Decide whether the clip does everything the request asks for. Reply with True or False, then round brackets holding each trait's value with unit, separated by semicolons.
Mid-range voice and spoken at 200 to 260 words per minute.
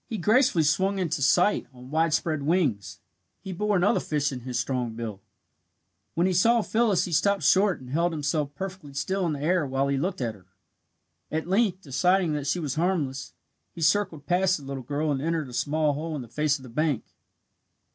True (155 Hz; 205 wpm)